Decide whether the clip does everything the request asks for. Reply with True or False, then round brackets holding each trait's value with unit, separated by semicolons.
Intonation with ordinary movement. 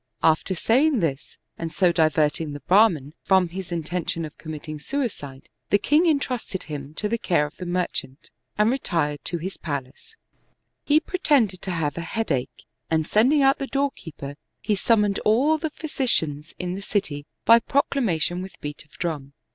False (7.1 semitones)